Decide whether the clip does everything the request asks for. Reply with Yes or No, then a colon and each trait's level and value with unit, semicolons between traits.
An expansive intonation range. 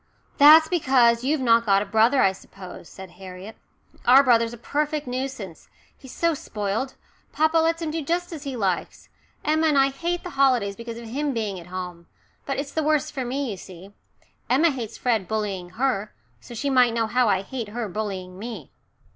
Yes: wide, 5.7 semitones